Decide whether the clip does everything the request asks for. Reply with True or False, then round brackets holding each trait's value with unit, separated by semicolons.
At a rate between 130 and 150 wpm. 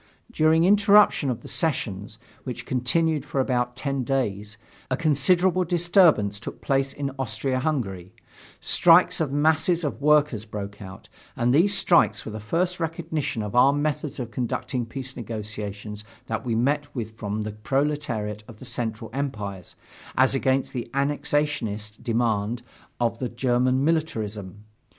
True (145 wpm)